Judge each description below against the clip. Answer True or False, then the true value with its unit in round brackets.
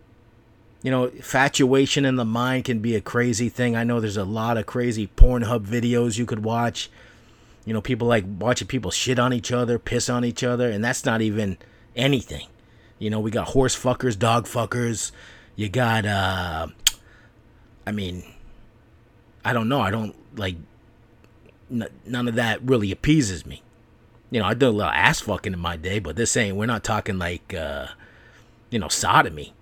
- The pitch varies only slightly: True (2.0 semitones)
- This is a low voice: True (115 Hz)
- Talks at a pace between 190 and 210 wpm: False (180 wpm)